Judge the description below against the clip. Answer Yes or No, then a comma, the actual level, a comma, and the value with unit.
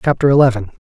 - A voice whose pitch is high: No, low, 125 Hz